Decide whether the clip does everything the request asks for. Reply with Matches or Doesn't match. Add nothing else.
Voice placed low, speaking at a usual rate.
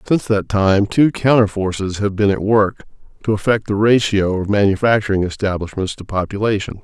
Matches